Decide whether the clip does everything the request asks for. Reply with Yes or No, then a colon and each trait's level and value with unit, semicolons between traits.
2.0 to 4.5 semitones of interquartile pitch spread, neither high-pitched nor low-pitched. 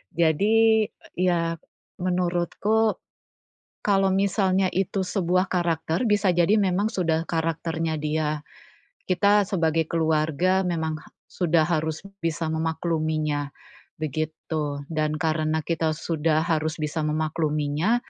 Yes: average, 2.8 semitones; medium, 165 Hz